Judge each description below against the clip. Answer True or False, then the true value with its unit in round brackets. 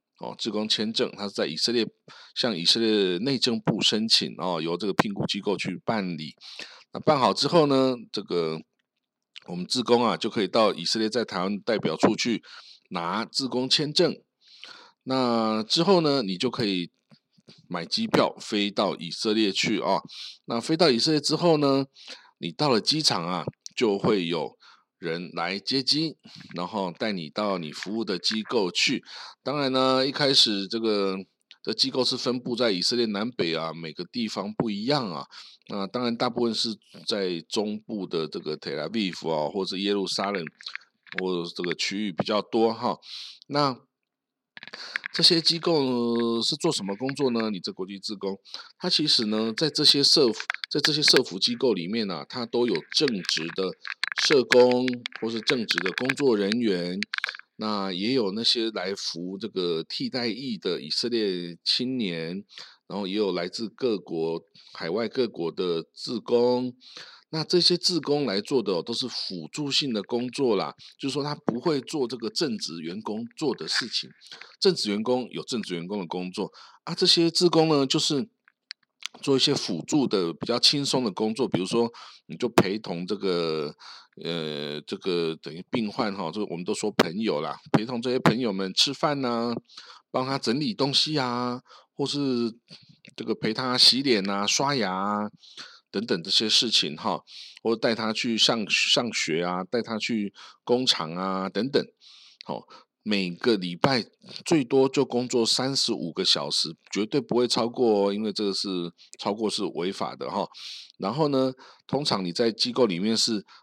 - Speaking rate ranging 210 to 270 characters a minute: True (245 characters per minute)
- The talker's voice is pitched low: True (120 Hz)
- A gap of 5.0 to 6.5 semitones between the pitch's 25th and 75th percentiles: True (5.6 semitones)